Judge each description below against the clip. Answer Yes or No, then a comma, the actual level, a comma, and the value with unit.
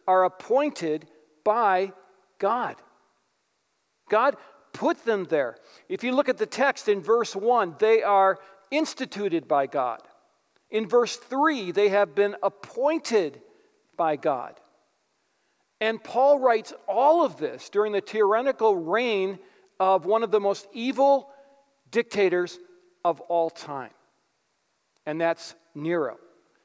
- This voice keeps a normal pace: No, slow, 120 wpm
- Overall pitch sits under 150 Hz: No, high, 210 Hz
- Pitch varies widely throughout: Yes, wide, 6.1 semitones